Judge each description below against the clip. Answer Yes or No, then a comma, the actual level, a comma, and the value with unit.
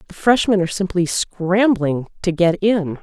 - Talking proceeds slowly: No, average, 160 wpm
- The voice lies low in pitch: No, medium, 185 Hz